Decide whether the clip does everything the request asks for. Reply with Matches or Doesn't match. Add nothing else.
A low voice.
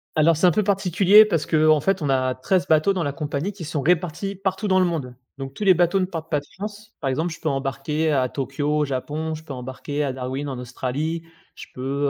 Doesn't match